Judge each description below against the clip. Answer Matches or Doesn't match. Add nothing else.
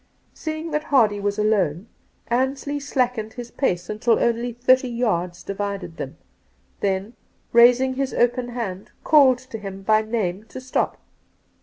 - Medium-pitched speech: Doesn't match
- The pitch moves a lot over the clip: Doesn't match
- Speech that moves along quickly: Doesn't match